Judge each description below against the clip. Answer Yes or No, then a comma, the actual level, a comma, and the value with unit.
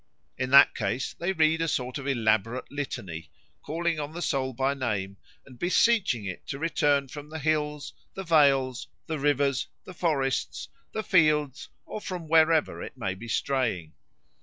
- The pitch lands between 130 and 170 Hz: Yes, medium, 140 Hz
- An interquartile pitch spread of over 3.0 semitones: Yes, average, 4.0 semitones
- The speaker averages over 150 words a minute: Yes, average, 160 wpm